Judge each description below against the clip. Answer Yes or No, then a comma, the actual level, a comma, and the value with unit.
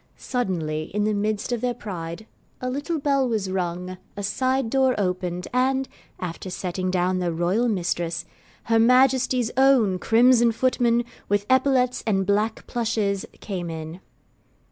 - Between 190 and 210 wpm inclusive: No, average, 145 wpm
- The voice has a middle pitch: No, high, 215 Hz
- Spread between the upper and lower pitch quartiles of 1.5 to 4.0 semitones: No, wide, 5.5 semitones